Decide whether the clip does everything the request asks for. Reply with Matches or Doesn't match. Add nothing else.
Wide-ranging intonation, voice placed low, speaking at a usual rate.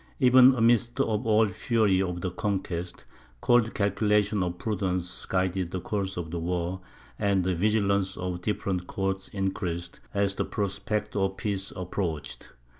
Doesn't match